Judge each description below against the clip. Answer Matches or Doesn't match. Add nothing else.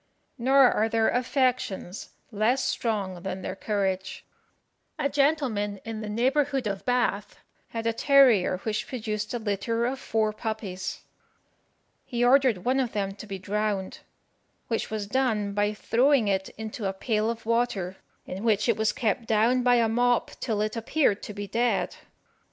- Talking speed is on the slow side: Doesn't match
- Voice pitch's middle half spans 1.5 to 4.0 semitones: Matches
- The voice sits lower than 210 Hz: Doesn't match